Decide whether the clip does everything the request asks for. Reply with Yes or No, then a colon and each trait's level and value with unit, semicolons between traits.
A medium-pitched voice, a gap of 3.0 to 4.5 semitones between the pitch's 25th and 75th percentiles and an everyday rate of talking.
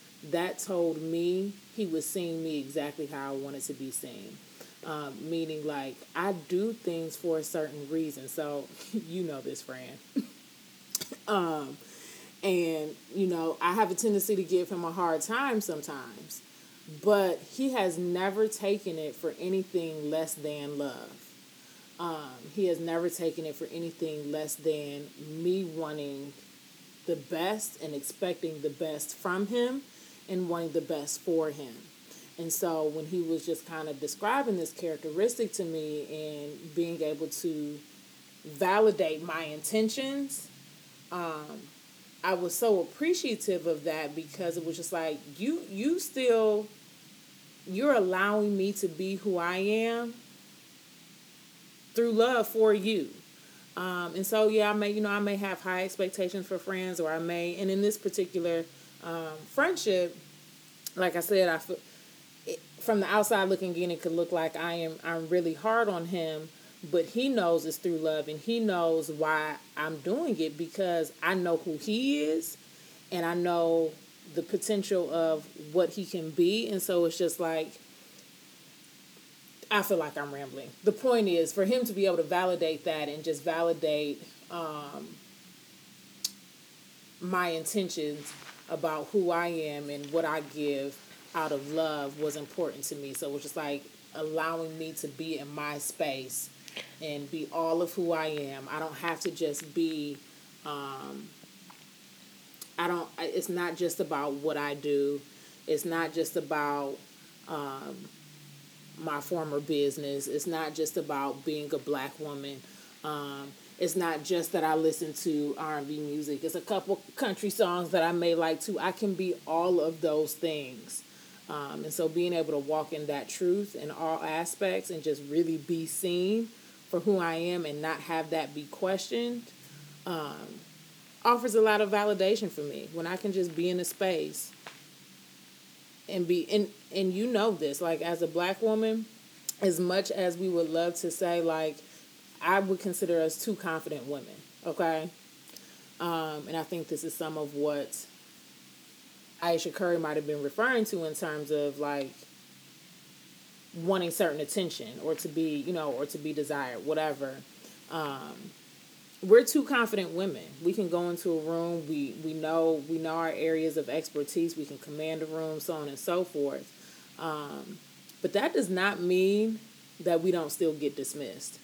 Yes: medium, 165 Hz; average, 3.4 semitones; average, 165 wpm